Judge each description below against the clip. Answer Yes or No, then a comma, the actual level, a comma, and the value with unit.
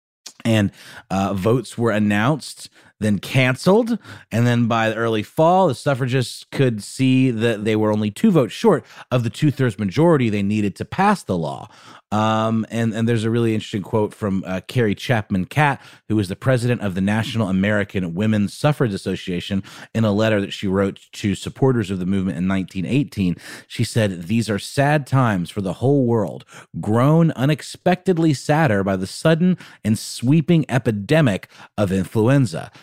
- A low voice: Yes, low, 115 Hz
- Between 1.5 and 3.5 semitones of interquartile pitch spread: No, average, 4.9 semitones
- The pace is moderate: Yes, average, 170 wpm